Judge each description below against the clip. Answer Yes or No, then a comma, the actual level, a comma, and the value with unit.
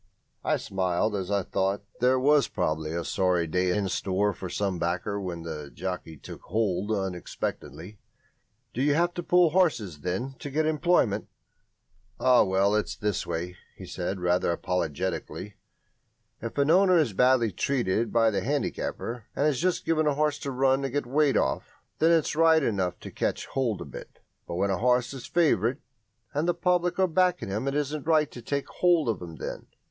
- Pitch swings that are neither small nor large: No, wide, 8.0 semitones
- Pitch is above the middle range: No, low, 115 Hz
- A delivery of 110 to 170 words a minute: No, average, 185 wpm